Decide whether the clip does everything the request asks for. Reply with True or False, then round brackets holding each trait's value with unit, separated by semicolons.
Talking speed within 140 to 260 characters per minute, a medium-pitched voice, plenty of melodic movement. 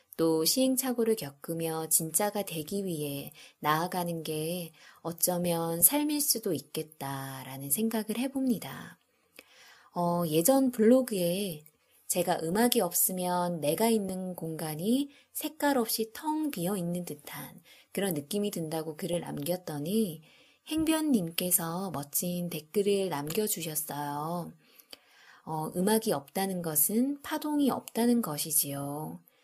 True (250 characters per minute; 180 Hz; 5.9 semitones)